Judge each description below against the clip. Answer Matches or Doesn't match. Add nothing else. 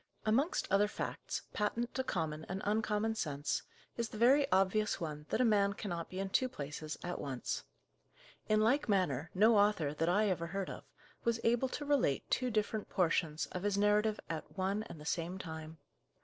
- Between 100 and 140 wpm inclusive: Doesn't match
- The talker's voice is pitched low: Doesn't match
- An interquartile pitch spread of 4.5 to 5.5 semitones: Matches